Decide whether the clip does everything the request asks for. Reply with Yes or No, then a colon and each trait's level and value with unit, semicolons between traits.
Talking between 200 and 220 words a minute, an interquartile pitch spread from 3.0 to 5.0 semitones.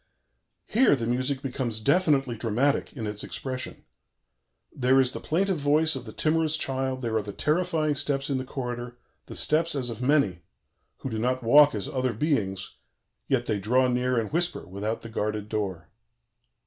No: average, 175 wpm; average, 4.2 semitones